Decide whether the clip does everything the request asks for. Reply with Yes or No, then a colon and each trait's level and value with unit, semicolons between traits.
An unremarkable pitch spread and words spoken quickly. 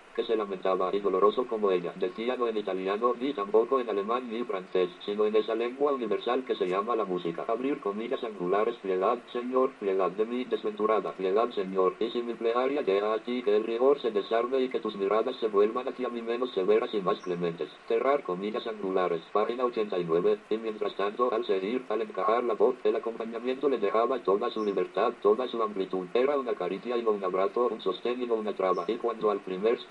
Yes: average, 4.2 semitones; fast, 210 wpm